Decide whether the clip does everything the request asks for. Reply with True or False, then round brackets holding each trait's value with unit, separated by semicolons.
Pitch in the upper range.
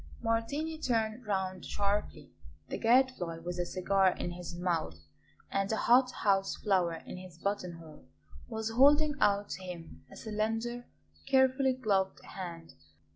True (200 Hz)